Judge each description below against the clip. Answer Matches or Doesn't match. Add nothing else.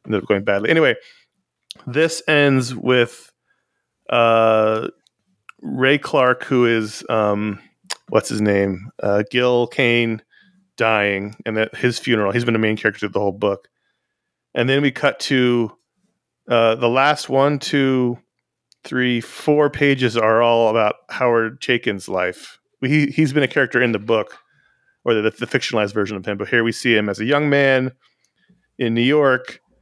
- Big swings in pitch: Doesn't match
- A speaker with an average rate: Matches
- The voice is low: Matches